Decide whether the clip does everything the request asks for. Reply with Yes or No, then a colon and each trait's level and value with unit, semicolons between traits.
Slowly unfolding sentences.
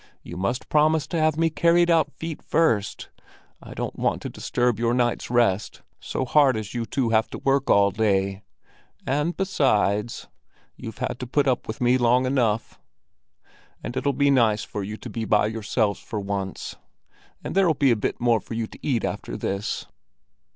No: average, 185 wpm